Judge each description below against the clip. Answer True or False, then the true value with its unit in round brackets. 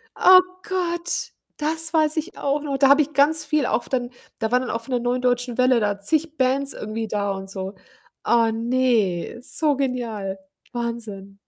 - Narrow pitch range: False (4.9 semitones)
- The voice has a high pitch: True (250 Hz)